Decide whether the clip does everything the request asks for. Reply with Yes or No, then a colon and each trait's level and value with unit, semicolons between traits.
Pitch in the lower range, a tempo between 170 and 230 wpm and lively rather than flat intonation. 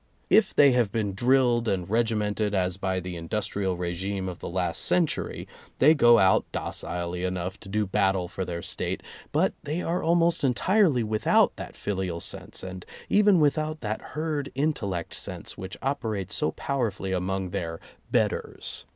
No: low, 105 Hz; average, 160 wpm; wide, 6.5 semitones